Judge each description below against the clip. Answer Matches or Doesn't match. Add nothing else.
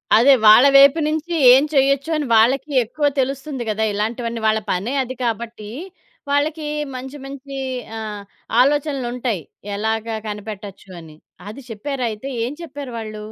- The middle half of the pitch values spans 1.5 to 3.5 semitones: Doesn't match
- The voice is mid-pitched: Doesn't match